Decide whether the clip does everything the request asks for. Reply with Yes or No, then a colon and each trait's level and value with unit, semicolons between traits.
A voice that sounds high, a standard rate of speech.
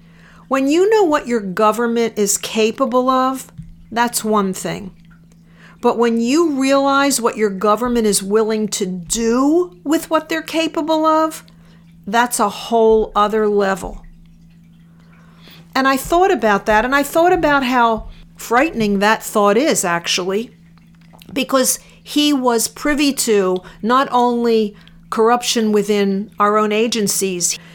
No: high, 220 Hz; slow, 130 wpm